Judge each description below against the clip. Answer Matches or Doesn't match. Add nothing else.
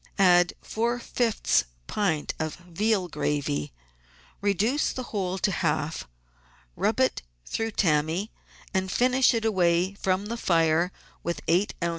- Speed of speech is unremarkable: Doesn't match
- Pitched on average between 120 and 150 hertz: Doesn't match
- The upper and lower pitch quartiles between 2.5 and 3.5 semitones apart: Doesn't match